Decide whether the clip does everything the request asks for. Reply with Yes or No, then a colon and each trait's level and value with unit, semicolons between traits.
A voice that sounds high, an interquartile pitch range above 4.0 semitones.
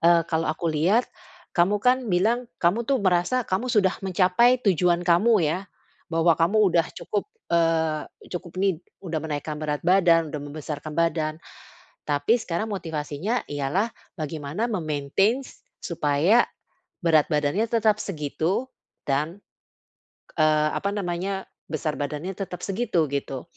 No: medium, 170 Hz; average, 4.4 semitones